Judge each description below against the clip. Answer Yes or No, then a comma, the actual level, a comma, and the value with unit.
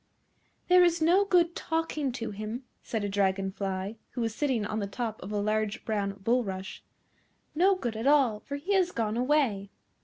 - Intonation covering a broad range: Yes, wide, 6.5 semitones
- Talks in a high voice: Yes, high, 230 Hz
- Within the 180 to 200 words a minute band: Yes, average, 185 wpm